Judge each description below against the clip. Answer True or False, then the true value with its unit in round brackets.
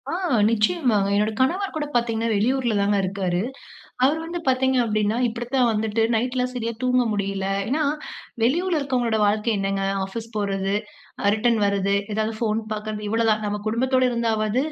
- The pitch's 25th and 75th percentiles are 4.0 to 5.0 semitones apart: False (3.3 semitones)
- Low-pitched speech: False (225 Hz)